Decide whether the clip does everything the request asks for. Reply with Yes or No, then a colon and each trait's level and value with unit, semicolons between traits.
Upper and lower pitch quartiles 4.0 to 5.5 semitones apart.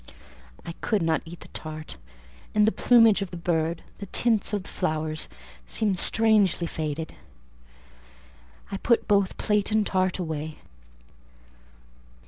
Yes: average, 4.6 semitones